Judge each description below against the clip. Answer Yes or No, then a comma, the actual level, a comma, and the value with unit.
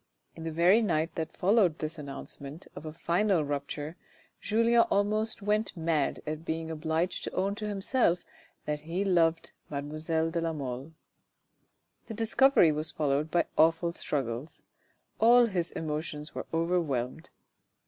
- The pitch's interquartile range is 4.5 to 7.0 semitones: No, average, 3.9 semitones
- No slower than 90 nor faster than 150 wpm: Yes, average, 140 wpm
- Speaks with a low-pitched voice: No, medium, 165 Hz